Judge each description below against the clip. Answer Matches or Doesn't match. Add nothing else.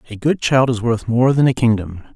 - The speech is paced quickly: Matches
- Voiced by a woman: Doesn't match